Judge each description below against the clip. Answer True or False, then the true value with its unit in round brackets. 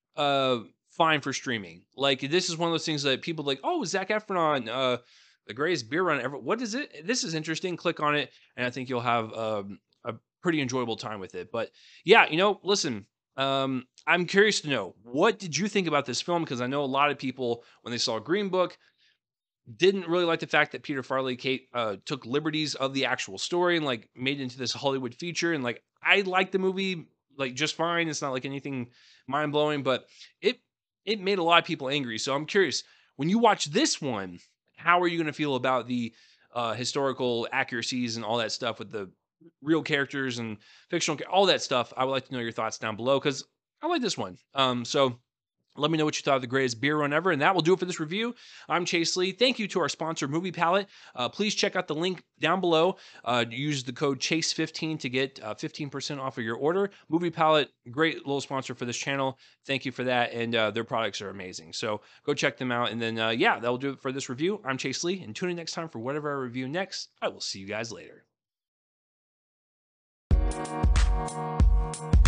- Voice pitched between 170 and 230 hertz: False (140 Hz)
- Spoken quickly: True (225 wpm)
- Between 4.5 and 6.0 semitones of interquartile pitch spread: True (5.2 semitones)